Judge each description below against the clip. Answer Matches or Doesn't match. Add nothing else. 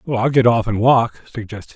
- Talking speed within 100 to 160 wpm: Doesn't match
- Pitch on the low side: Matches